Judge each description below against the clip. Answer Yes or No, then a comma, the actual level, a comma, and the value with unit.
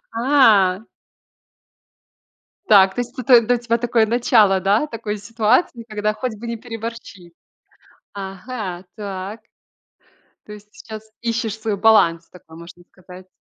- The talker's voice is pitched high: Yes, high, 215 Hz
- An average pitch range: Yes, average, 3.3 semitones